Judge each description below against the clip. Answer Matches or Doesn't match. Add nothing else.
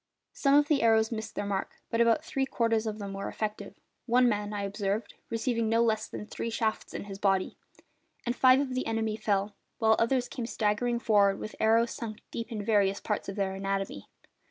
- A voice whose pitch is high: Matches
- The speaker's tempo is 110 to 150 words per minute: Doesn't match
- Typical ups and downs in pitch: Doesn't match